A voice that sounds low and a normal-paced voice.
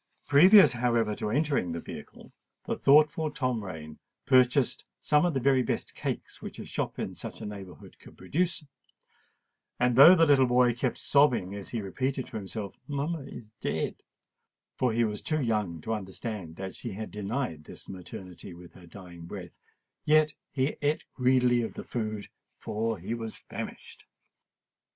Yes: low, 120 Hz; average, 160 wpm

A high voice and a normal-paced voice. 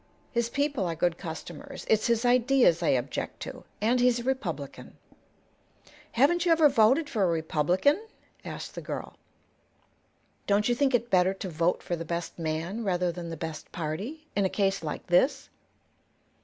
Yes: high, 195 Hz; average, 170 wpm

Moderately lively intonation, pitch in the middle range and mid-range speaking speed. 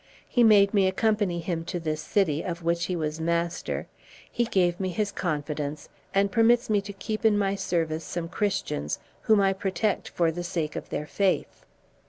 Yes: average, 3.6 semitones; medium, 180 Hz; average, 185 wpm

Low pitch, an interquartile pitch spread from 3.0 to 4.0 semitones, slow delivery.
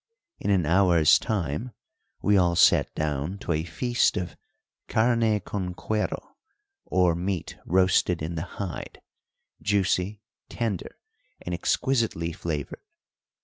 Yes: very low, 90 Hz; average, 3.6 semitones; slow, 115 wpm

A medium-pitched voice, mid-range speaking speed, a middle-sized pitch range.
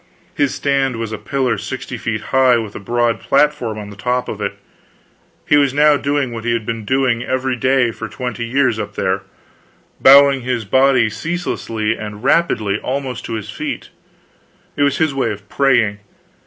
No: low, 125 Hz; average, 180 wpm; average, 3.6 semitones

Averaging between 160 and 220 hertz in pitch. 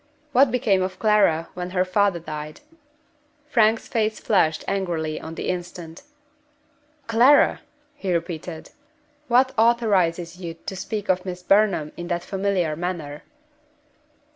Yes: medium, 185 Hz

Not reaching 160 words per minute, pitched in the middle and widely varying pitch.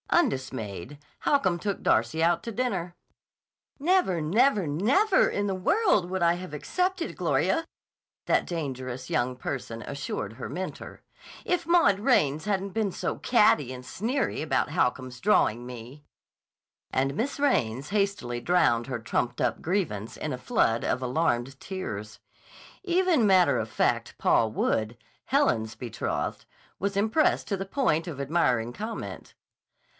Yes: average, 140 wpm; medium, 170 Hz; wide, 9.0 semitones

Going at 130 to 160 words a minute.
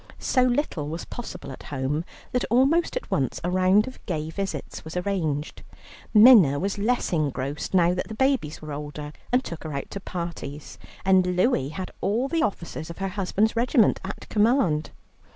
No: average, 175 wpm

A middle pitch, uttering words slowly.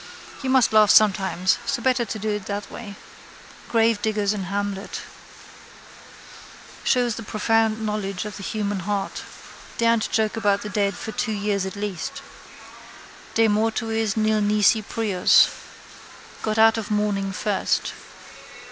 No: high, 210 Hz; slow, 130 wpm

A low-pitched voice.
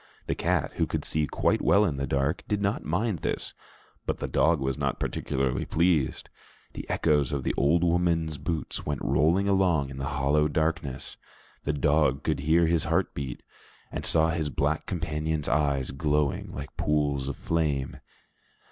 Yes: very low, 75 Hz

